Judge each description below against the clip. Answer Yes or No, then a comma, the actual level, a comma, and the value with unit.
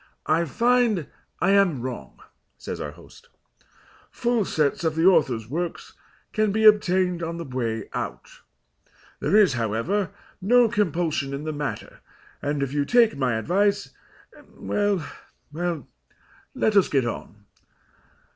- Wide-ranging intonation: Yes, wide, 6.7 semitones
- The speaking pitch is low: No, medium, 170 Hz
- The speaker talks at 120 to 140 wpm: Yes, slow, 135 wpm